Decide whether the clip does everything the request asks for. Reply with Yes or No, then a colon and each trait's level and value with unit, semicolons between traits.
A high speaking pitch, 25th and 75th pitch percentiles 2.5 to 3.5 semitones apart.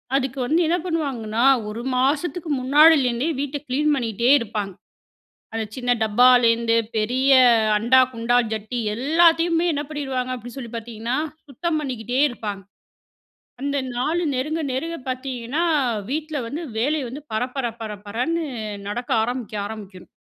No: very high, 255 Hz; average, 4.3 semitones